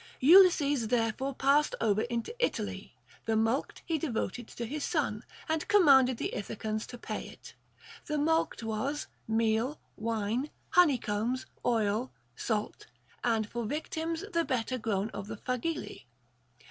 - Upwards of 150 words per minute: No, average, 140 wpm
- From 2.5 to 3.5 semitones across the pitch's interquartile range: No, average, 5.1 semitones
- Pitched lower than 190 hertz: No, high, 245 Hz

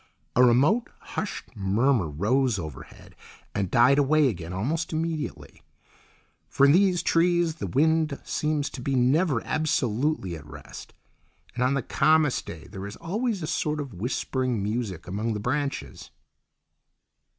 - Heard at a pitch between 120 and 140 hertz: Yes, low, 135 Hz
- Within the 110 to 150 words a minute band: Yes, average, 140 wpm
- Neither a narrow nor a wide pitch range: No, wide, 6.7 semitones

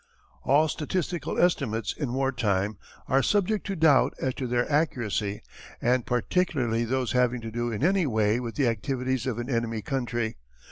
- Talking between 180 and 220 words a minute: No, average, 170 wpm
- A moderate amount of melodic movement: Yes, average, 3.7 semitones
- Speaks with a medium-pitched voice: No, low, 125 Hz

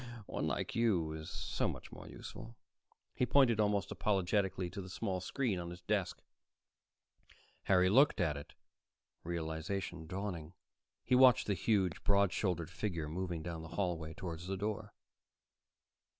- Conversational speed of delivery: Yes, average, 150 wpm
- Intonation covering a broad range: No, average, 3.4 semitones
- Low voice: Yes, very low, 95 Hz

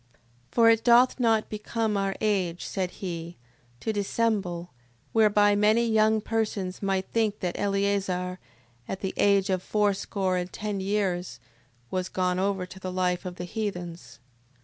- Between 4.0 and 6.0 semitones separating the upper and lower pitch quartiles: No, average, 2.7 semitones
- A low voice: No, high, 195 Hz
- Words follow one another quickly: No, average, 155 wpm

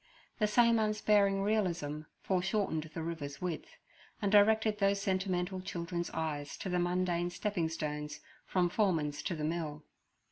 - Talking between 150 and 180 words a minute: No, average, 140 wpm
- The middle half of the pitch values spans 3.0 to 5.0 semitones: Yes, average, 3.8 semitones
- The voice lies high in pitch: No, medium, 180 Hz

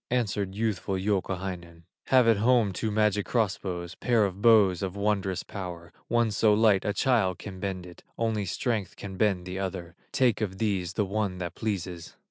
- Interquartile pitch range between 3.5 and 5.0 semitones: No, average, 2.9 semitones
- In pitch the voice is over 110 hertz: No, low, 100 Hz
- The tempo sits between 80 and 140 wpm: No, average, 180 wpm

